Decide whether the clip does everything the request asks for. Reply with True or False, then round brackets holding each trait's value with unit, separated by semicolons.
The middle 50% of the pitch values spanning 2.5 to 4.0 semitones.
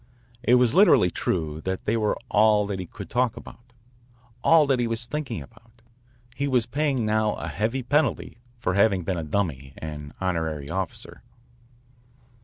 False (5.4 semitones)